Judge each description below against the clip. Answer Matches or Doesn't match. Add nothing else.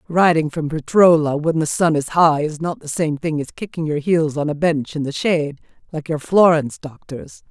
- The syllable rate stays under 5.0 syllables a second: Doesn't match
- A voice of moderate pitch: Matches